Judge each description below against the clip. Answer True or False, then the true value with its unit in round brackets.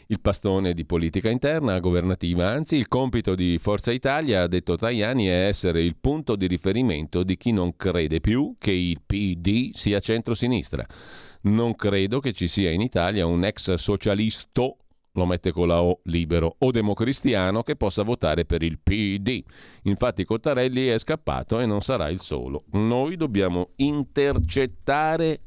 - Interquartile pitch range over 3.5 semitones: True (5.1 semitones)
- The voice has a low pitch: True (100 Hz)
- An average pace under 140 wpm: False (160 wpm)